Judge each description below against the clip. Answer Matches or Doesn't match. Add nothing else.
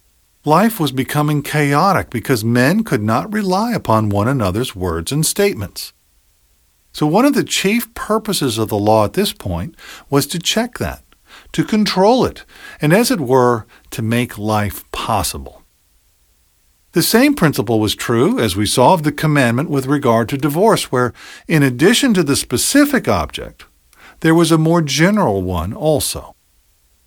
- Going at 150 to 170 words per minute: Matches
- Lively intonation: Matches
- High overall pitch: Doesn't match